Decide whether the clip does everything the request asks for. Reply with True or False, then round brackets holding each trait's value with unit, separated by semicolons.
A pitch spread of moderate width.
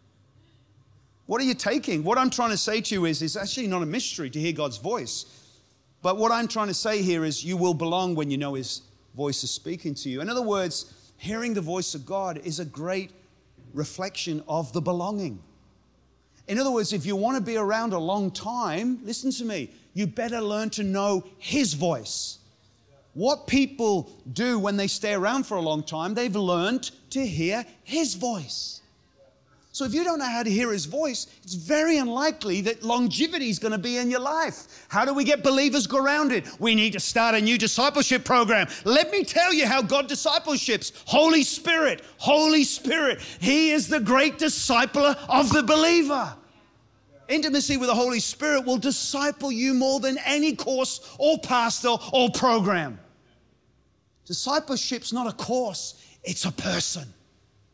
False (7.7 semitones)